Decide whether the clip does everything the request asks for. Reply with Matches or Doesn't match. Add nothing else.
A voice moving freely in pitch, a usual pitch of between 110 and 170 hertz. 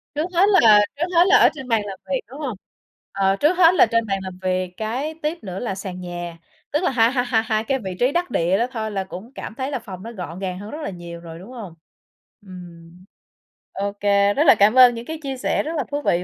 Doesn't match